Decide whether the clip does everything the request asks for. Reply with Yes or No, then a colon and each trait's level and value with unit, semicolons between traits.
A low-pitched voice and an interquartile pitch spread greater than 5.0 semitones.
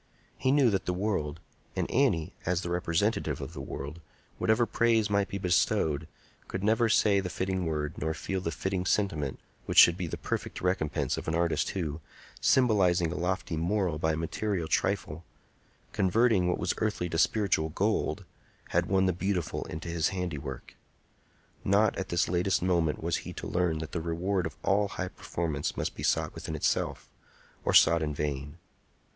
No: very low, 90 Hz; average, 3.6 semitones